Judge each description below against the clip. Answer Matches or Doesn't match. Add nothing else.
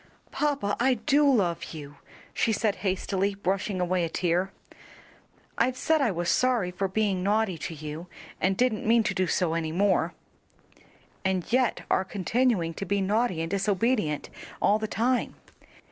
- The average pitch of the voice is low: Doesn't match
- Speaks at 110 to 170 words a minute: Matches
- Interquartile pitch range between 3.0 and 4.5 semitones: Matches